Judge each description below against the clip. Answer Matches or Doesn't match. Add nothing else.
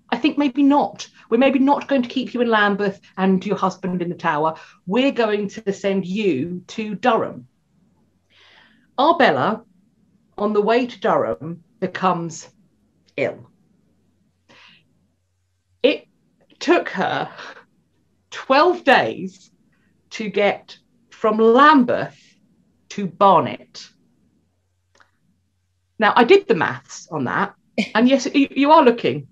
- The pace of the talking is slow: Matches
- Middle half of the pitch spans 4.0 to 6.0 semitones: Matches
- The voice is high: Matches